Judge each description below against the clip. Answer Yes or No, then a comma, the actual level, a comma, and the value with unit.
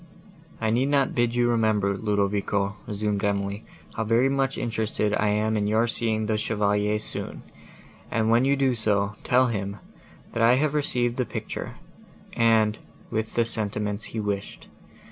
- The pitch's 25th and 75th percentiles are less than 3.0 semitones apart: Yes, narrow, 2.4 semitones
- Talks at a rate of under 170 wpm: Yes, average, 160 wpm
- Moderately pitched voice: No, low, 110 Hz